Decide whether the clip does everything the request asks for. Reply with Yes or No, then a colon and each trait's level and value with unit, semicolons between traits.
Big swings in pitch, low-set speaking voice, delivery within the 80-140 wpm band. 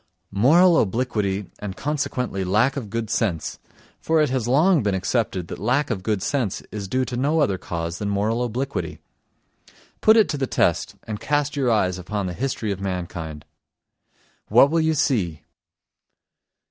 No: wide, 6.3 semitones; low, 115 Hz; average, 165 wpm